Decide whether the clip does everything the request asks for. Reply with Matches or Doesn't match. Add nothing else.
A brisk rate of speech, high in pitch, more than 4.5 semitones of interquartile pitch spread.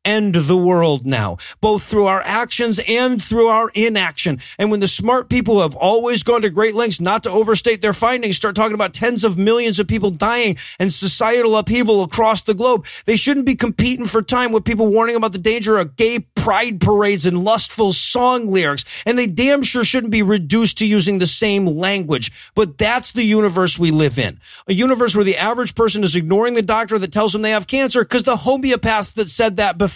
Doesn't match